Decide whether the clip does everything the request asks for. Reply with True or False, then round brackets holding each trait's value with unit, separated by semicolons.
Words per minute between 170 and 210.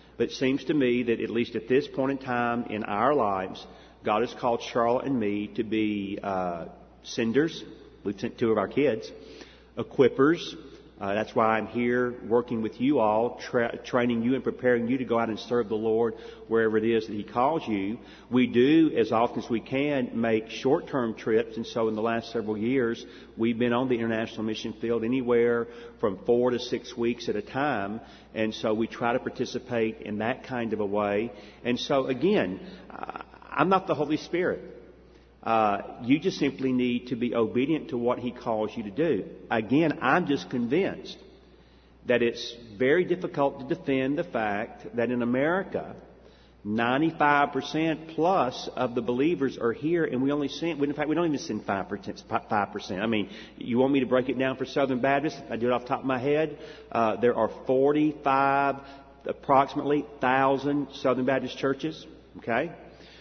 True (185 wpm)